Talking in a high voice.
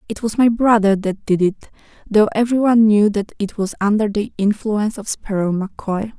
Yes: high, 210 Hz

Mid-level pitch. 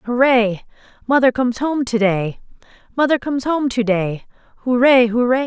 No: high, 245 Hz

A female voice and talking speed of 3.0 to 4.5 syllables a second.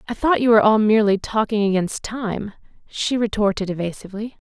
No: female; 5.9 syllables/s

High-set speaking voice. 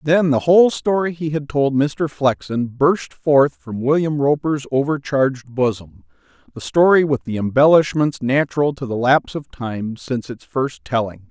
No: medium, 140 Hz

